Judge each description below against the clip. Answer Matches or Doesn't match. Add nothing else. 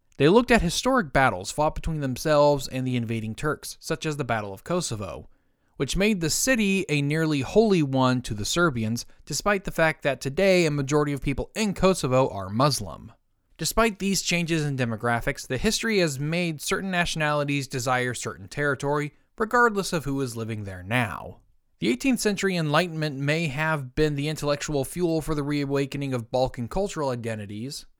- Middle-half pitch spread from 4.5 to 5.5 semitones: Matches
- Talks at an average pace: Matches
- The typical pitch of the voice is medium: Matches